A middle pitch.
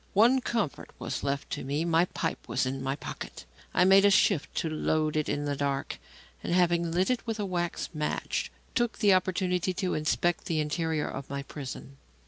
Yes: medium, 170 Hz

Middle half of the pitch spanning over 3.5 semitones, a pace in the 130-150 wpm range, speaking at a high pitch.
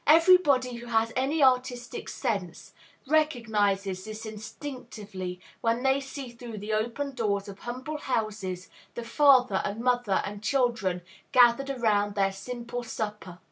Yes: average, 3.9 semitones; slow, 135 wpm; high, 235 Hz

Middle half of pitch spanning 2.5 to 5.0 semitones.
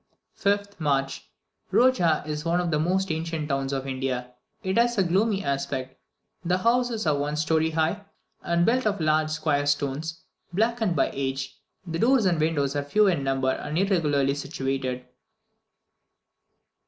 No: wide, 5.4 semitones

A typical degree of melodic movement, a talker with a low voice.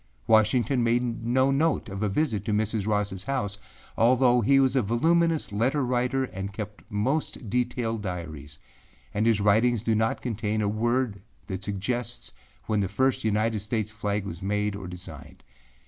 Yes: average, 3.3 semitones; low, 110 Hz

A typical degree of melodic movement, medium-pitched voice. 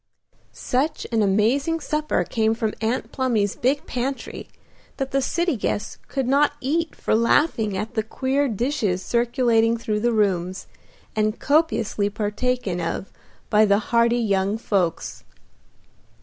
No: average, 4.2 semitones; high, 230 Hz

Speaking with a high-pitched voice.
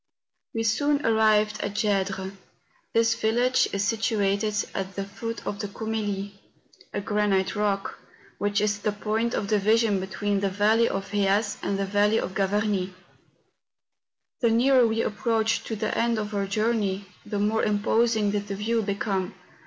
Yes: high, 210 Hz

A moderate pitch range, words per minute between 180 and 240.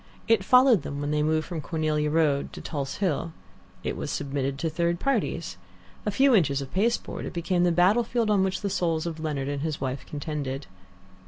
Yes: average, 4.7 semitones; average, 195 wpm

